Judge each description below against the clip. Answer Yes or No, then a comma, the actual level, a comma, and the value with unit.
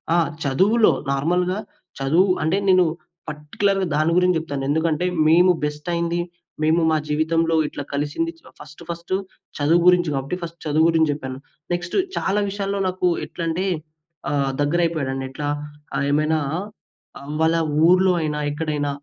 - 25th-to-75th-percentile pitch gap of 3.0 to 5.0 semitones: Yes, average, 3.3 semitones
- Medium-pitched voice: Yes, medium, 165 Hz